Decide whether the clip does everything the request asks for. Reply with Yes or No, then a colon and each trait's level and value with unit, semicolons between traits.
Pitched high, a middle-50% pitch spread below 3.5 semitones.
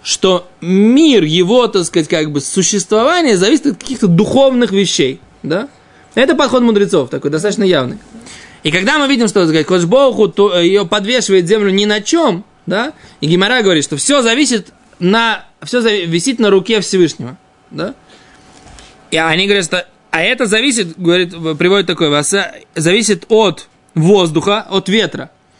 No: high, 200 Hz; average, 4.2 semitones